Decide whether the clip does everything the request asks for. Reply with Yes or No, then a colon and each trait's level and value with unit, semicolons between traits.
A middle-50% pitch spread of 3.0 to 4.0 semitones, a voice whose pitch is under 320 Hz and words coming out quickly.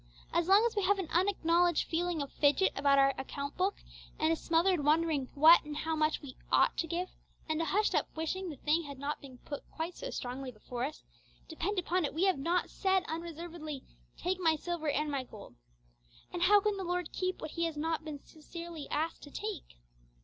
No: average, 3.3 semitones; very high, 325 Hz; fast, 210 wpm